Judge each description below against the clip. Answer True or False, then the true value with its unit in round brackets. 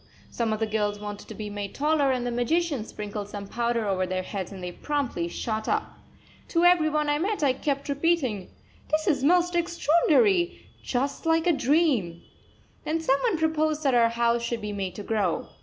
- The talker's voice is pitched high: True (260 Hz)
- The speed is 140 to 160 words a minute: False (195 wpm)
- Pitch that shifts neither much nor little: False (7.1 semitones)